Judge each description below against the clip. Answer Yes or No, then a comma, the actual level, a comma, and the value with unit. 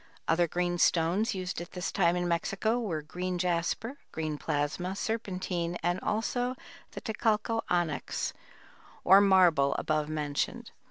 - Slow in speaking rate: Yes, slow, 130 wpm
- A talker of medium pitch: Yes, medium, 180 Hz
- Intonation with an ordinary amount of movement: Yes, average, 3.1 semitones